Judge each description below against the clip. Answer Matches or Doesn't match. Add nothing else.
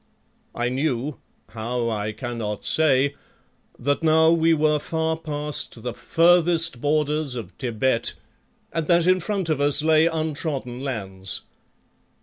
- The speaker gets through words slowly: Matches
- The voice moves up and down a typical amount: Matches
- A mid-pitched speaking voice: Matches